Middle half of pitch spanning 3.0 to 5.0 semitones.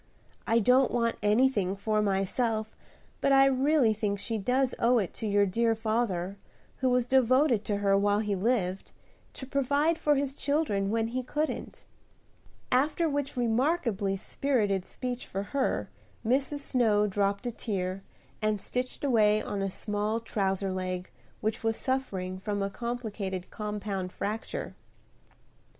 Yes: average, 4.3 semitones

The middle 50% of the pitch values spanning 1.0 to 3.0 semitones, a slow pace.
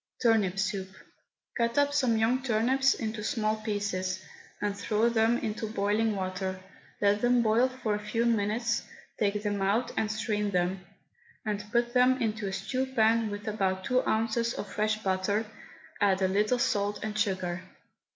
No: narrow, 2.6 semitones; average, 160 wpm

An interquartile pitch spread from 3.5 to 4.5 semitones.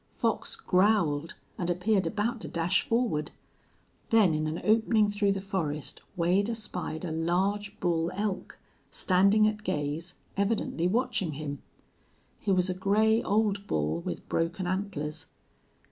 Yes: average, 4.1 semitones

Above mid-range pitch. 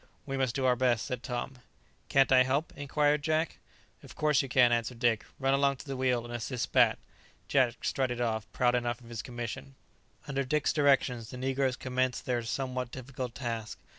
No: low, 130 Hz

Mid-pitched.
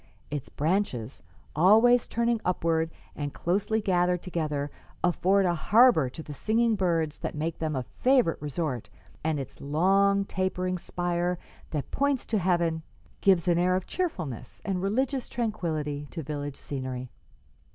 Yes: medium, 175 Hz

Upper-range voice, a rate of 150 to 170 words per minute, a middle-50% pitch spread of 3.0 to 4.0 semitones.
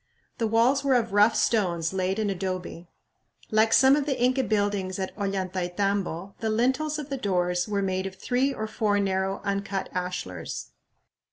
Yes: high, 200 Hz; average, 165 wpm; average, 3.5 semitones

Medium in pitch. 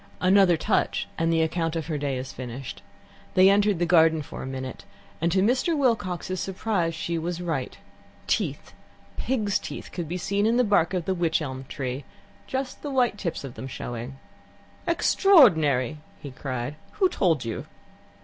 Yes: medium, 170 Hz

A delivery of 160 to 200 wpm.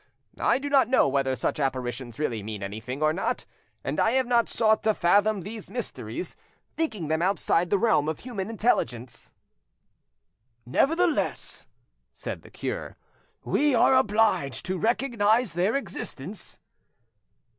No: slow, 135 wpm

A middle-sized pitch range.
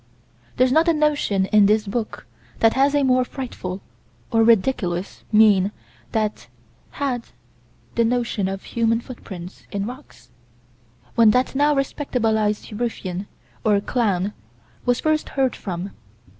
Yes: average, 4.2 semitones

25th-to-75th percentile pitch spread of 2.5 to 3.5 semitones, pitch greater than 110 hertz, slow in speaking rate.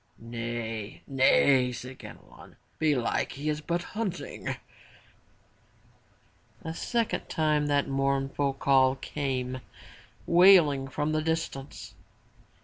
Yes: average, 3.0 semitones; medium, 140 Hz; slow, 105 wpm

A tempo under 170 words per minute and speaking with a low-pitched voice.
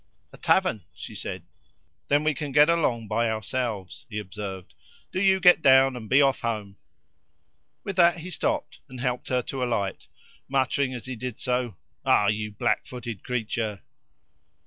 Yes: average, 160 wpm; low, 125 Hz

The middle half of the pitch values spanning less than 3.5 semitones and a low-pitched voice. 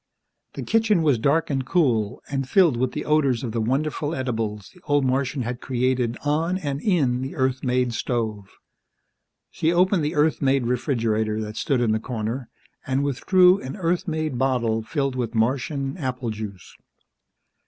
No: average, 4.2 semitones; low, 130 Hz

